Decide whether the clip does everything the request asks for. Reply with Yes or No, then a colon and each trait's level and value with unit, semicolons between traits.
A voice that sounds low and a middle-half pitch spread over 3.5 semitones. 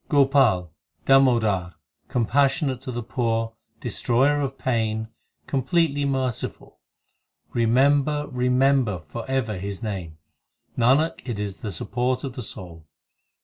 Yes: low, 125 Hz; average, 4.0 semitones